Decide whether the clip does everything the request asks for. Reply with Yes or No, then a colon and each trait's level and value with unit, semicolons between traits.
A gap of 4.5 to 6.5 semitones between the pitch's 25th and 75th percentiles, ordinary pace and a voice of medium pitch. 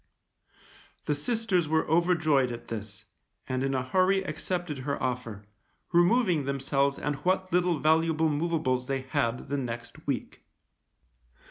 No: average, 4.9 semitones; slow, 130 wpm; medium, 150 Hz